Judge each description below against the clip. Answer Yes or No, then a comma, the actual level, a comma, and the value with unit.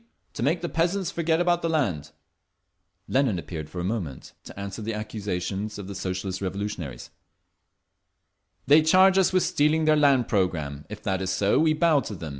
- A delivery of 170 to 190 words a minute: Yes, average, 180 wpm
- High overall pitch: No, low, 105 Hz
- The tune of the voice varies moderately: No, wide, 9.0 semitones